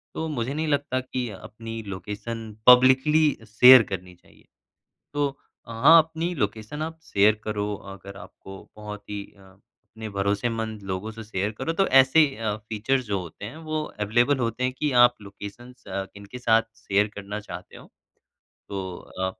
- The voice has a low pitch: Yes, low, 110 Hz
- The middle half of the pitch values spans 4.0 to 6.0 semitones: Yes, average, 4.3 semitones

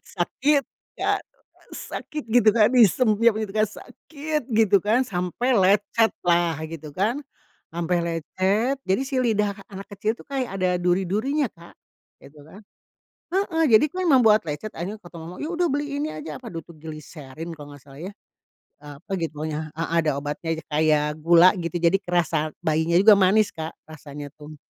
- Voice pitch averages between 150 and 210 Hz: Yes, medium, 185 Hz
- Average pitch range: No, wide, 5.9 semitones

